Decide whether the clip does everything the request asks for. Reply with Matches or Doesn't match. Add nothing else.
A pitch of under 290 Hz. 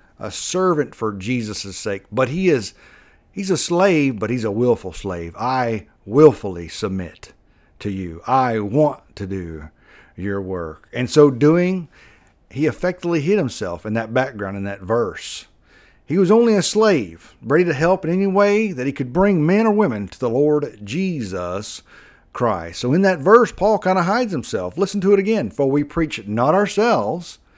Matches